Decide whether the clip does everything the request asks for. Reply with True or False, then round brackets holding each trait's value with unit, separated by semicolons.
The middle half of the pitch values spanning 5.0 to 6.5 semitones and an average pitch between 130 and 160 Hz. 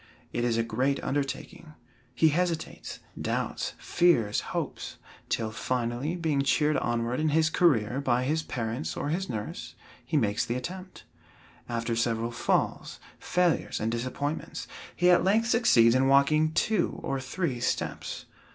True (5.4 semitones; 135 Hz)